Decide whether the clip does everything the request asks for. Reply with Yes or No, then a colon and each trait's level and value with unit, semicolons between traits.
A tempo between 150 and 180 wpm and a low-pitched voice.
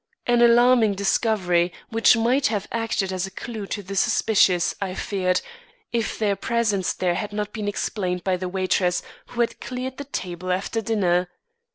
No: average, 170 wpm; high, 205 Hz